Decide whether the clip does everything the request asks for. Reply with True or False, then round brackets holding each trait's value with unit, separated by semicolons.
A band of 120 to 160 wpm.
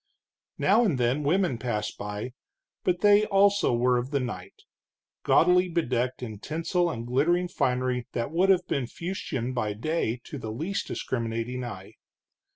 True (150 wpm)